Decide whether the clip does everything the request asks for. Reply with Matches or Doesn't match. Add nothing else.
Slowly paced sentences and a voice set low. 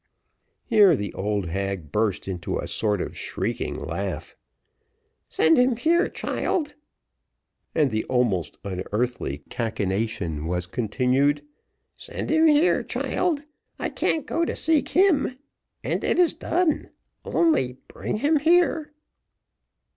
Matches